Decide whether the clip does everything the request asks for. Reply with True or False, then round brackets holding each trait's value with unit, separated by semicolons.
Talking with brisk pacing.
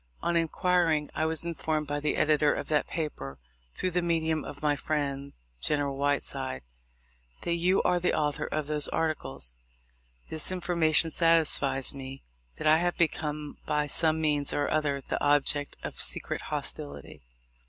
False (155 wpm)